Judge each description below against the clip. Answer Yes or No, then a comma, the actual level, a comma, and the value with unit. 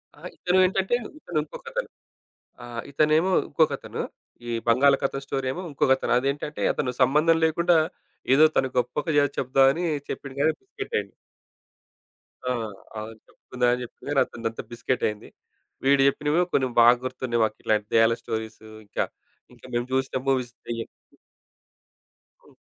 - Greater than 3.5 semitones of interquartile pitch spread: Yes, average, 4.2 semitones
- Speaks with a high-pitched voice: No, low, 135 Hz